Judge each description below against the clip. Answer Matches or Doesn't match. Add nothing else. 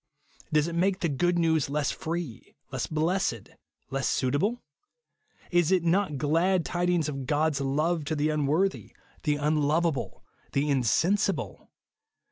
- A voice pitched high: Doesn't match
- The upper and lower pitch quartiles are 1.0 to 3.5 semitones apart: Matches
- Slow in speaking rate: Matches